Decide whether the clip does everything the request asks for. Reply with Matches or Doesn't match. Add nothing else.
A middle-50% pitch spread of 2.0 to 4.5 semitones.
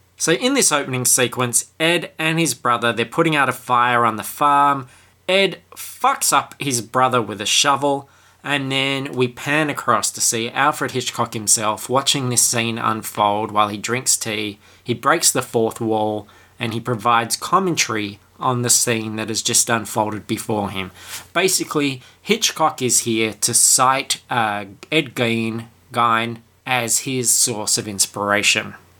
Matches